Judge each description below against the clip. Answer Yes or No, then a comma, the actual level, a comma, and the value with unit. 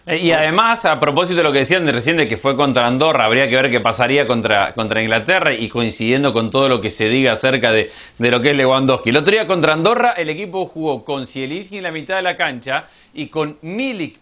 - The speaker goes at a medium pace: No, fast, 240 wpm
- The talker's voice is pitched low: No, medium, 145 Hz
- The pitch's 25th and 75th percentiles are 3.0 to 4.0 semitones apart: No, average, 5.2 semitones